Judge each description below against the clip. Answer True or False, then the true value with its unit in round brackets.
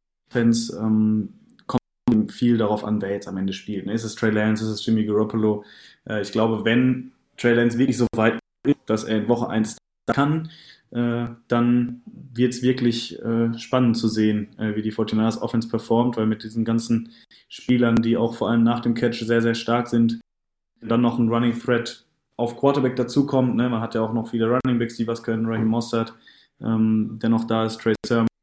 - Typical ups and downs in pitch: False (1.4 semitones)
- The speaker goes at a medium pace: False (200 wpm)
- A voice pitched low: True (115 Hz)